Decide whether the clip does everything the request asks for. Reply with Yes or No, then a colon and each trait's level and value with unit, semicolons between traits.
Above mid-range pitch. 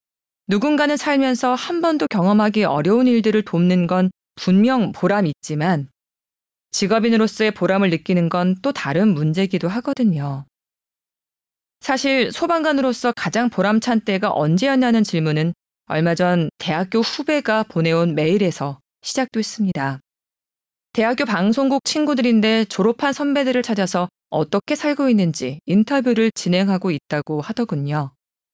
Yes: high, 205 Hz